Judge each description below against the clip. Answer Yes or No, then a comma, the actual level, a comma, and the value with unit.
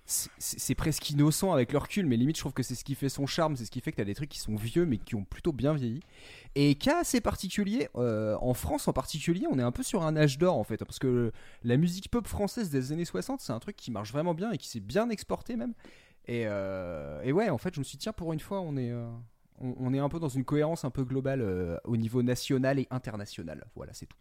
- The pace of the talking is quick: Yes, fast, 280 wpm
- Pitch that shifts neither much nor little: No, wide, 5.8 semitones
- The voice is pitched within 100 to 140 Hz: Yes, low, 135 Hz